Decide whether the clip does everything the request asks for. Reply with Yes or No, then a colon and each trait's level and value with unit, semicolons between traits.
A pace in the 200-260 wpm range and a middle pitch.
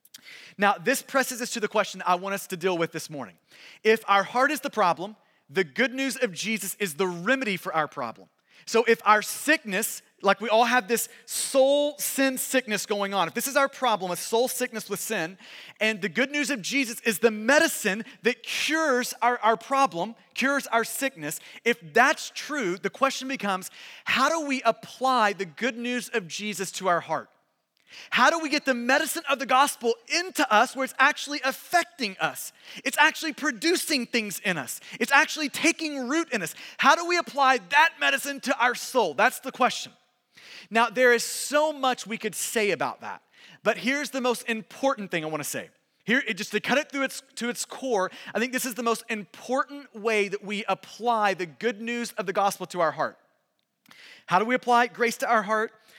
No: fast, 205 wpm; high, 235 Hz